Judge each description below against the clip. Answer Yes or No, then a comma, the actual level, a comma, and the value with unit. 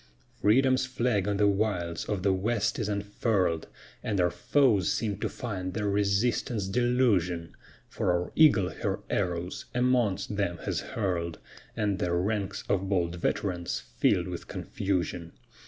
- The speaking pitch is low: Yes, low, 100 Hz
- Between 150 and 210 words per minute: No, average, 140 wpm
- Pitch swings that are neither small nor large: Yes, average, 3.6 semitones